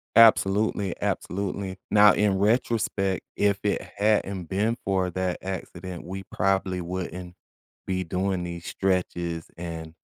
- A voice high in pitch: No, very low, 95 Hz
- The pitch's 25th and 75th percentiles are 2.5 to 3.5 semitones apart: No, narrow, 1.9 semitones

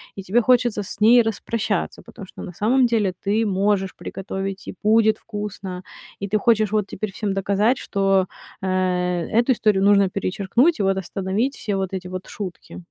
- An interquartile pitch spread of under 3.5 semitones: Yes, narrow, 2.4 semitones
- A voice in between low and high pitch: No, high, 200 Hz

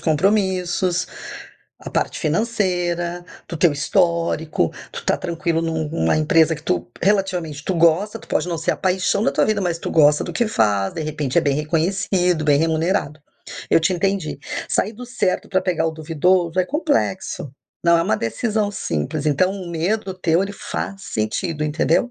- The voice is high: No, medium, 170 Hz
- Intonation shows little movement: No, average, 3.4 semitones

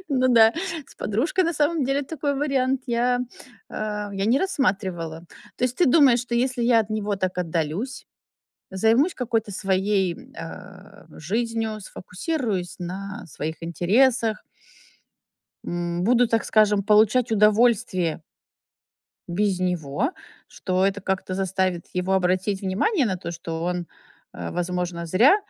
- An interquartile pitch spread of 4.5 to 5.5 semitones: Yes, average, 5.2 semitones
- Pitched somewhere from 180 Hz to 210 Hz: Yes, high, 205 Hz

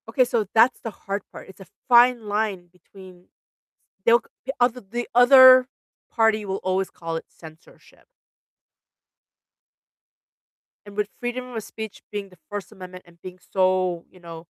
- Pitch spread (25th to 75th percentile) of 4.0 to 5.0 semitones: Yes, average, 4.5 semitones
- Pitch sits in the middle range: No, high, 205 Hz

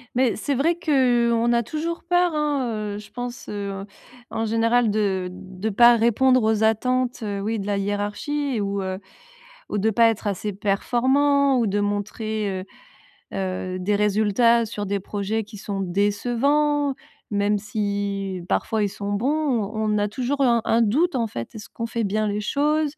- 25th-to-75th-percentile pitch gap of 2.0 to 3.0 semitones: No, average, 3.6 semitones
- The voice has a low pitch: No, high, 220 Hz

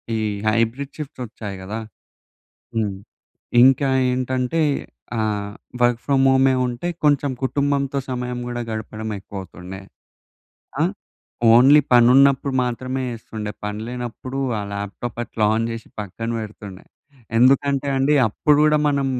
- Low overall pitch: Yes, low, 125 Hz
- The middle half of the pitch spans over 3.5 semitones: Yes, average, 3.9 semitones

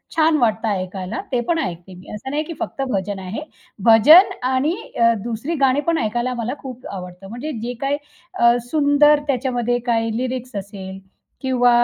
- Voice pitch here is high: Yes, high, 240 Hz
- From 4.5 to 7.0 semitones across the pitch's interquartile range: Yes, average, 4.8 semitones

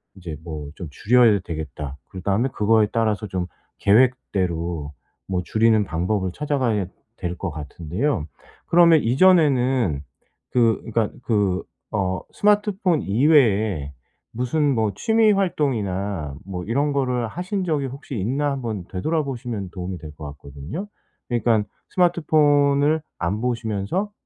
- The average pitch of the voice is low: Yes, low, 110 Hz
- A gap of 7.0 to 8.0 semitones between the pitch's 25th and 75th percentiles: Yes, wide, 7.5 semitones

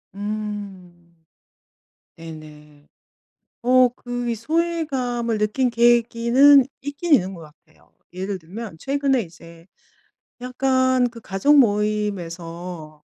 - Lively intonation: Yes, wide, 6.3 semitones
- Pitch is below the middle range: No, high, 215 Hz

